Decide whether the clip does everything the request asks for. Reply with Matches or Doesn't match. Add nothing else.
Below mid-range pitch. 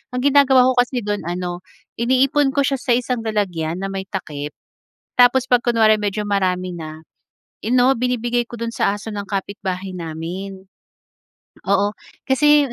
Doesn't match